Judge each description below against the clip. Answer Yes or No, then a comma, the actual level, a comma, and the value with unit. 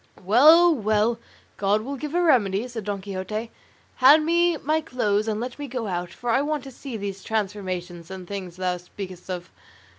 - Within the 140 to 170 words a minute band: No, average, 185 wpm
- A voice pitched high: Yes, high, 215 Hz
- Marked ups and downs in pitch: Yes, wide, 6.0 semitones